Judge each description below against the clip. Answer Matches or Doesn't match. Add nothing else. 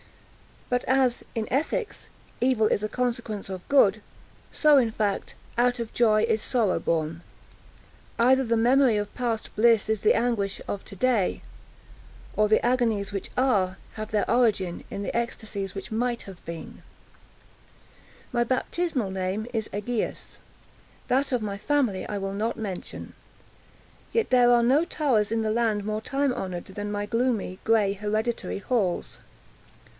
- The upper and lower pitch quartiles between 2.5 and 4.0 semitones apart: Matches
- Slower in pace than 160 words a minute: Matches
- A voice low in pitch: Doesn't match